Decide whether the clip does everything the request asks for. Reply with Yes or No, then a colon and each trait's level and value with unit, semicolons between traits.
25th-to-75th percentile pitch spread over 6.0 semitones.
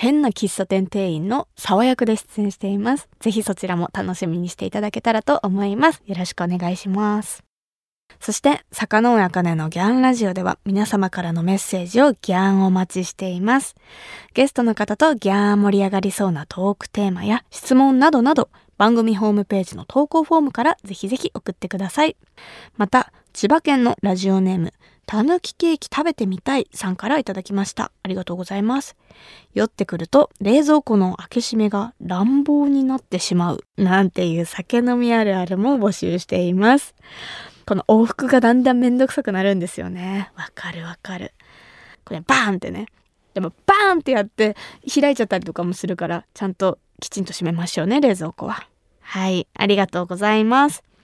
No: average, 5.3 semitones